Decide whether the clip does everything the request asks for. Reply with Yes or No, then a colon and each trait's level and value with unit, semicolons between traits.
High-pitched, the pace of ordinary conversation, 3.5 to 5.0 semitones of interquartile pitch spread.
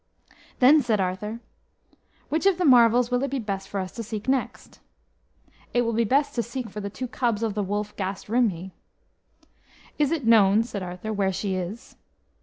Yes: high, 220 Hz; average, 190 wpm; average, 3.8 semitones